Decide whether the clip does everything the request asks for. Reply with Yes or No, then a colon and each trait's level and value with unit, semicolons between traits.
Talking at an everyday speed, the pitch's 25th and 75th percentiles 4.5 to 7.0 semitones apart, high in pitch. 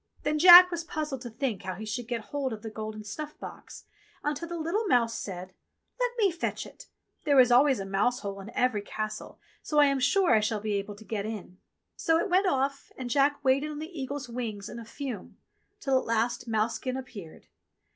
No: fast, 215 wpm; wide, 5.5 semitones; very high, 250 Hz